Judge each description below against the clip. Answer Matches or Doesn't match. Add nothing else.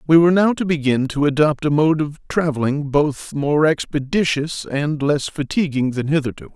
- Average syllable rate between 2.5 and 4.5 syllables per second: Doesn't match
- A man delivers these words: Matches